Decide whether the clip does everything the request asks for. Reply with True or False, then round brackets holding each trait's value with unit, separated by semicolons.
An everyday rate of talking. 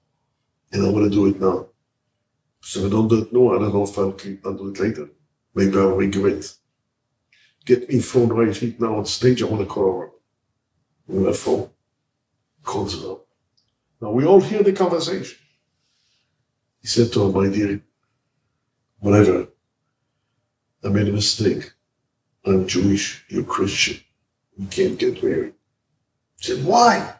True (150 wpm)